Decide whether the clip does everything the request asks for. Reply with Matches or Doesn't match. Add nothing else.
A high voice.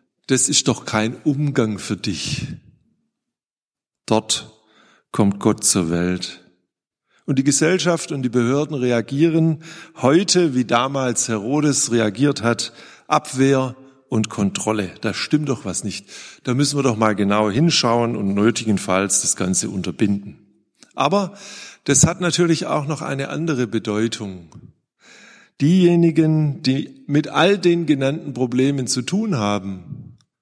Doesn't match